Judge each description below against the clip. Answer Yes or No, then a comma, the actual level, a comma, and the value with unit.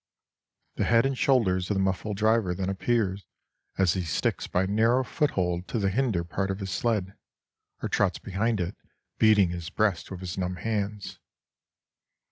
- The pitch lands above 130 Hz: No, very low, 95 Hz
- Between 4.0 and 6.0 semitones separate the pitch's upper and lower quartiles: No, average, 3.3 semitones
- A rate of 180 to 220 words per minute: No, average, 165 wpm